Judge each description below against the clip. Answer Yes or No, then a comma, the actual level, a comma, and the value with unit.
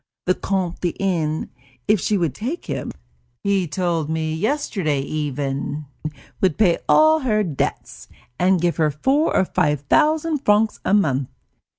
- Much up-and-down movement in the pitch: Yes, wide, 5.8 semitones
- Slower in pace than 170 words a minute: Yes, average, 150 wpm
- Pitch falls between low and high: Yes, medium, 180 Hz